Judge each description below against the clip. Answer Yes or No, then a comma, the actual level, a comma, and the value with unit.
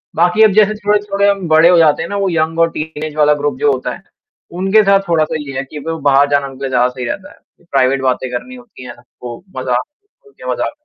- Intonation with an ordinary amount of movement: No, wide, 6.1 semitones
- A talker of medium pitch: Yes, medium, 155 Hz